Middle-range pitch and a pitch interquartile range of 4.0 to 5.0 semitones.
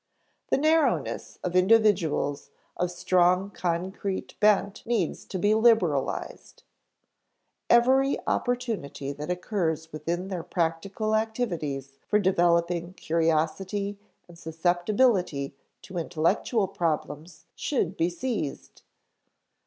Yes: medium, 180 Hz; average, 4.4 semitones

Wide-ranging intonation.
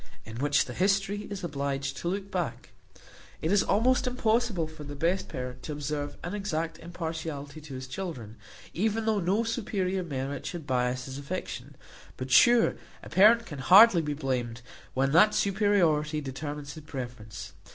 Yes: wide, 6.2 semitones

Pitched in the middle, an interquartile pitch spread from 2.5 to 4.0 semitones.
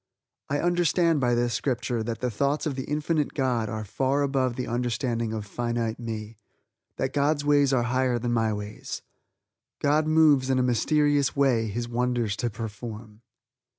No: low, 125 Hz; average, 3.7 semitones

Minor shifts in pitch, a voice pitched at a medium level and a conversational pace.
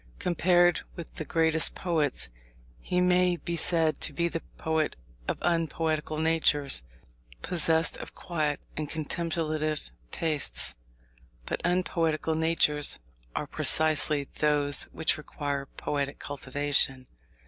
No: narrow, 2.2 semitones; medium, 160 Hz; slow, 110 wpm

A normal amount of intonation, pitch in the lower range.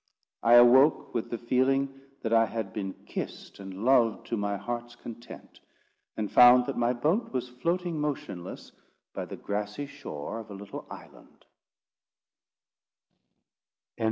Yes: average, 4.1 semitones; low, 120 Hz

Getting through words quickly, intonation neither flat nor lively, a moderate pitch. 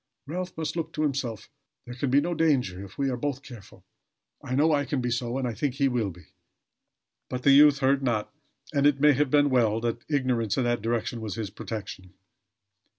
No: fast, 215 wpm; average, 3.7 semitones; low, 130 Hz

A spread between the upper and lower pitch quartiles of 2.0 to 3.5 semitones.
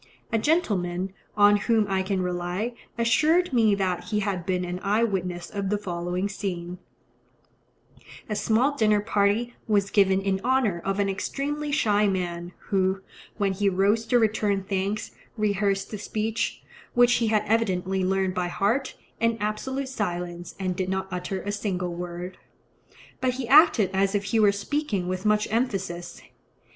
Yes: average, 3.1 semitones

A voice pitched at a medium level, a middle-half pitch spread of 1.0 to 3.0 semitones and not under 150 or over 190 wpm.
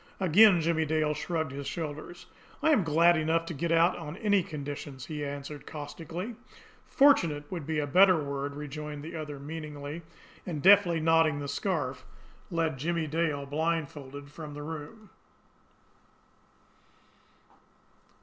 No: medium, 155 Hz; narrow, 2.6 semitones; slow, 135 wpm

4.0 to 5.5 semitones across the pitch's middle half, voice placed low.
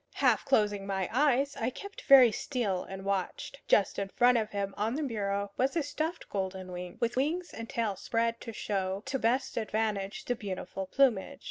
No: average, 4.8 semitones; high, 220 Hz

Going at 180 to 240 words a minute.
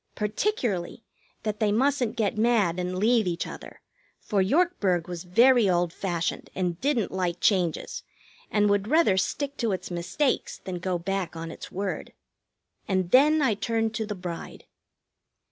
No: average, 155 wpm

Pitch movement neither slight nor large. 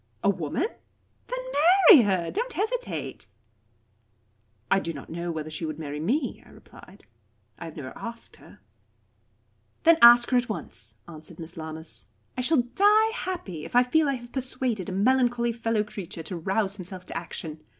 No: wide, 8.0 semitones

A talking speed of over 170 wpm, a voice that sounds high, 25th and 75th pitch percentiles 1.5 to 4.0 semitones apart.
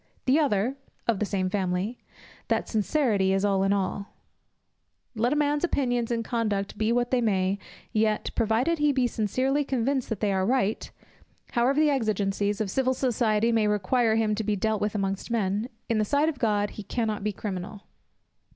Yes: average, 180 wpm; high, 220 Hz; average, 3.7 semitones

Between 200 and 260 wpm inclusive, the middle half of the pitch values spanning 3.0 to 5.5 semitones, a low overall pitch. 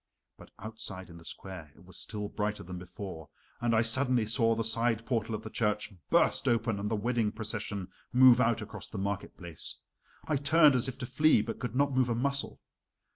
Yes: fast, 205 wpm; average, 3.5 semitones; low, 115 Hz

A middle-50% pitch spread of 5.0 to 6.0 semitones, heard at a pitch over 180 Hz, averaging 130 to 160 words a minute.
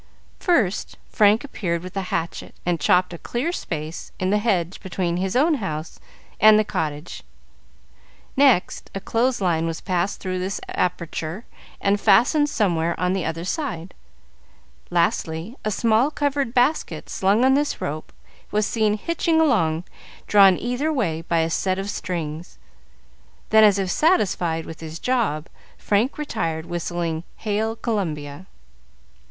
Yes: wide, 5.4 semitones; high, 190 Hz; average, 145 wpm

